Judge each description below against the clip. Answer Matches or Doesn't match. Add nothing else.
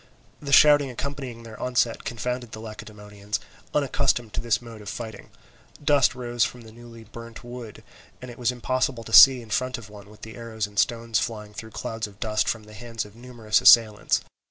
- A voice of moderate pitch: Doesn't match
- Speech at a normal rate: Matches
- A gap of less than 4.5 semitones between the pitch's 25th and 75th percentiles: Matches